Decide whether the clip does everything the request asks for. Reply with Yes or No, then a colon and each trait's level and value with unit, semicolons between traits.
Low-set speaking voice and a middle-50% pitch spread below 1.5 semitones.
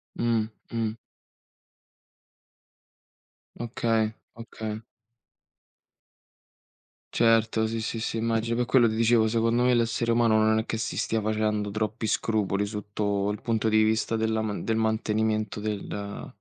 Yes: low, 110 Hz; narrow, 1.1 semitones